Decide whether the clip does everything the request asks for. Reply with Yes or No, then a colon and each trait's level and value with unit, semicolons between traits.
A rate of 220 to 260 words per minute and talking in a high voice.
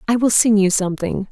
Yes: fast, 230 wpm; high, 205 Hz